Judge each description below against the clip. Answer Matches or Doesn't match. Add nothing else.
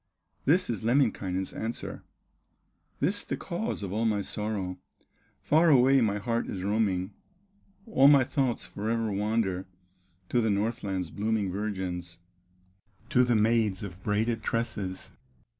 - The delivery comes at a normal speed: Doesn't match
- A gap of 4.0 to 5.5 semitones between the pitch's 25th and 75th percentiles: Doesn't match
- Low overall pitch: Matches